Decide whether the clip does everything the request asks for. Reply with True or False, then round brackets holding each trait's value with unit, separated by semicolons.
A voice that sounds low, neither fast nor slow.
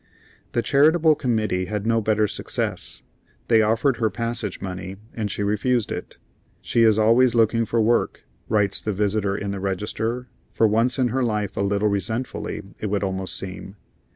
True (110 Hz; 170 wpm)